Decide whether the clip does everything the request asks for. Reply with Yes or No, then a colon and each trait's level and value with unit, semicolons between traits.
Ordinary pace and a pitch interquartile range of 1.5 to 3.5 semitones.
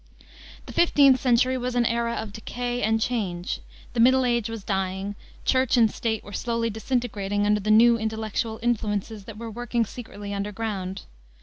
Yes: average, 170 wpm; average, 2.7 semitones